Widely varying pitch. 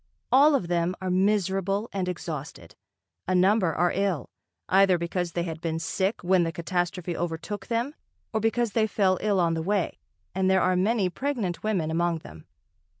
No: average, 3.0 semitones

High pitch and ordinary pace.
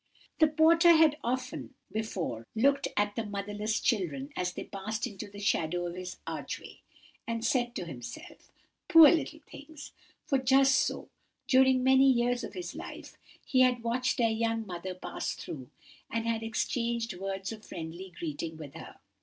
Yes: high, 225 Hz; average, 160 wpm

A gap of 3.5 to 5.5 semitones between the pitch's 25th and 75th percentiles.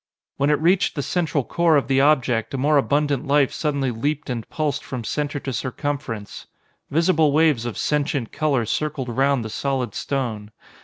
No: average, 3.0 semitones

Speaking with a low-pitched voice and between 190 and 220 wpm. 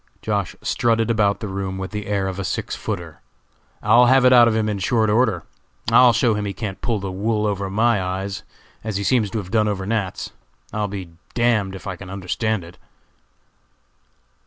Yes: low, 105 Hz; fast, 205 wpm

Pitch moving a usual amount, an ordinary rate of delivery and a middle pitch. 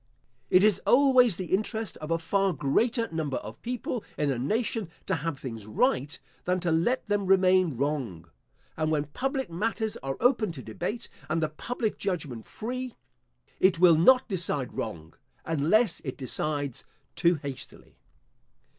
No: wide, 7.3 semitones; average, 155 wpm; medium, 170 Hz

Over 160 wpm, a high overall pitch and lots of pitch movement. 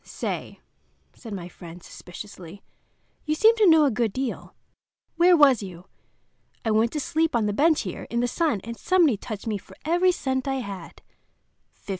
Yes: average, 175 wpm; high, 240 Hz; wide, 7.5 semitones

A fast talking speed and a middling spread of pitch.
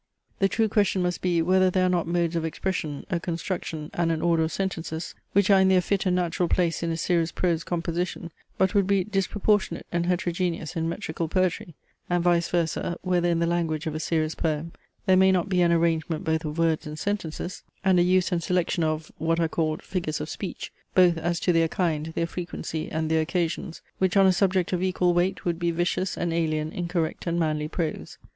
No: fast, 215 wpm; narrow, 2.0 semitones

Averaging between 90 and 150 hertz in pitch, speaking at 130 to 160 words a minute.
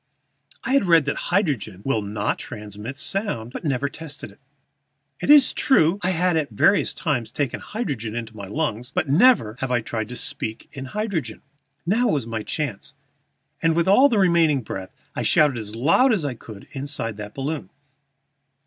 No: medium, 140 Hz; average, 180 wpm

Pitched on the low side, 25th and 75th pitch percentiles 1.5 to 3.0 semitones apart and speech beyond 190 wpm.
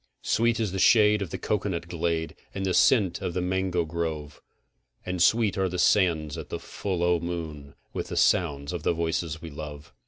Yes: very low, 85 Hz; average, 2.7 semitones; fast, 205 wpm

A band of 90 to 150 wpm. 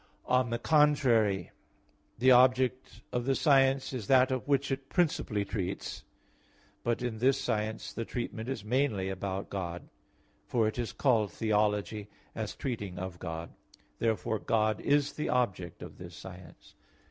Yes: average, 145 wpm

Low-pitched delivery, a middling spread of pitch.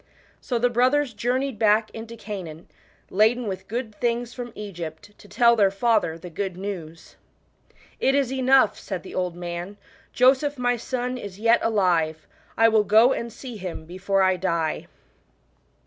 No: high, 215 Hz; average, 4.7 semitones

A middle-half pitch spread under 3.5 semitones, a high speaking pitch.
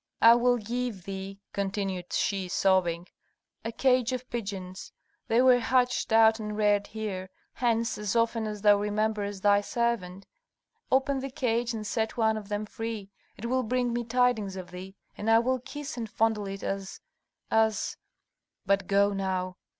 Yes: average, 3.1 semitones; high, 215 Hz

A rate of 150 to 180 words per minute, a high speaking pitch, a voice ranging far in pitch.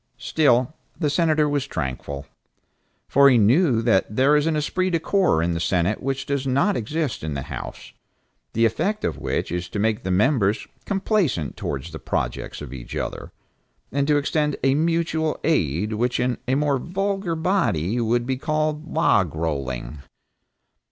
No: average, 165 wpm; low, 130 Hz; wide, 8.7 semitones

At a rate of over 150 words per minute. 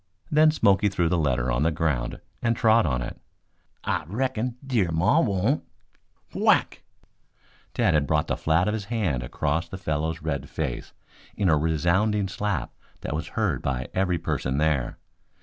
Yes: average, 165 wpm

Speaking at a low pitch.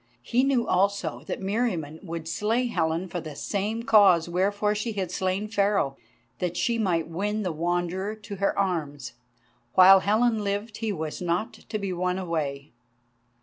No: high, 190 Hz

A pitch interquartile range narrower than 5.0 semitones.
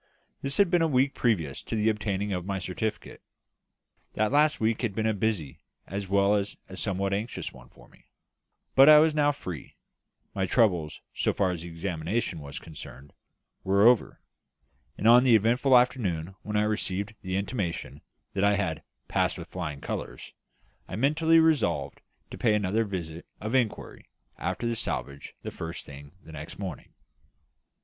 No: average, 5.3 semitones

